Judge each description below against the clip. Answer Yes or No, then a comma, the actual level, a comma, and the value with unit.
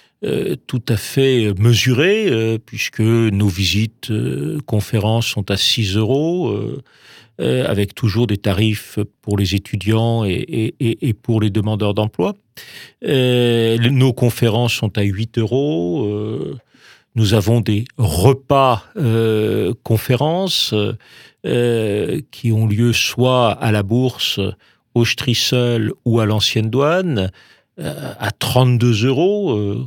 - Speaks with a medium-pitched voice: No, low, 115 Hz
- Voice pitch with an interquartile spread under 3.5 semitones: Yes, average, 2.9 semitones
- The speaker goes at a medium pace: No, slow, 125 wpm